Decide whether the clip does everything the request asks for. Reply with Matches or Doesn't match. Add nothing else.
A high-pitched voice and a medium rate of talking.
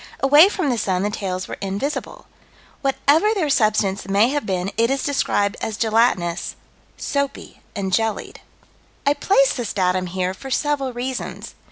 Matches